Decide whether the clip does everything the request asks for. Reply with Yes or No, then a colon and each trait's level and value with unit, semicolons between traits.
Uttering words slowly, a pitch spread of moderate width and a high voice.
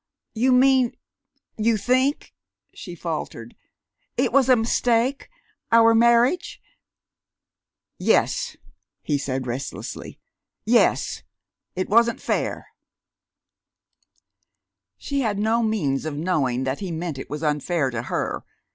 No: slow, 110 wpm; wide, 8.2 semitones; high, 220 Hz